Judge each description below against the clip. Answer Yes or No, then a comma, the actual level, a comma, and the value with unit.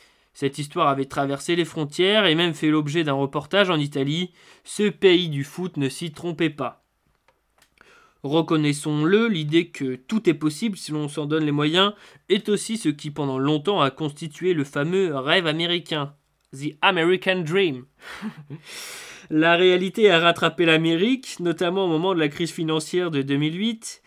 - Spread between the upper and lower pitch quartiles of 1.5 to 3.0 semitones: No, average, 3.8 semitones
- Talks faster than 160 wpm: No, average, 155 wpm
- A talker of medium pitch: Yes, medium, 165 Hz